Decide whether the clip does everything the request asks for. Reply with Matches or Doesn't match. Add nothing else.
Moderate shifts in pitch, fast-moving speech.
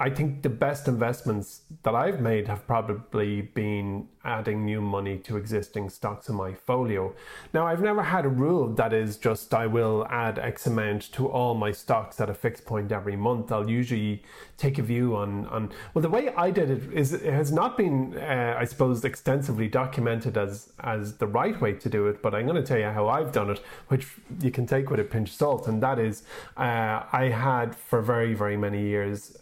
Matches